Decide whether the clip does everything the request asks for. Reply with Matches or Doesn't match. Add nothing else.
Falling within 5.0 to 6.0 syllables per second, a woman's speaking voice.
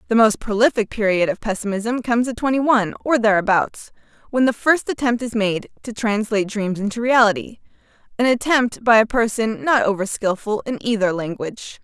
Matches